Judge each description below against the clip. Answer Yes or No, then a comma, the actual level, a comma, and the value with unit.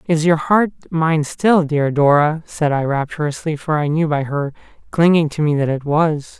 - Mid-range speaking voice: Yes, medium, 155 Hz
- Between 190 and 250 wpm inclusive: Yes, average, 195 wpm